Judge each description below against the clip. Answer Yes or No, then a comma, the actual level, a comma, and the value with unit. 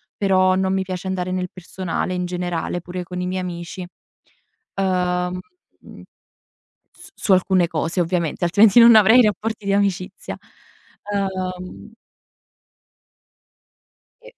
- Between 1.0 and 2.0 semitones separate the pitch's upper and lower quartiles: Yes, narrow, 1.5 semitones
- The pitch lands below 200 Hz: Yes, medium, 185 Hz